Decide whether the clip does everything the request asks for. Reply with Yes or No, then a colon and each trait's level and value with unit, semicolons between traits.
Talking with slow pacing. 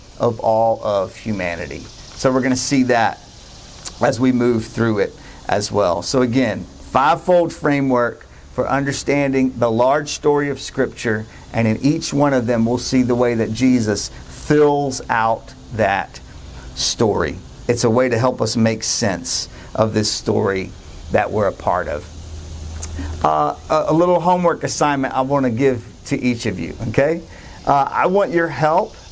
No: average, 165 wpm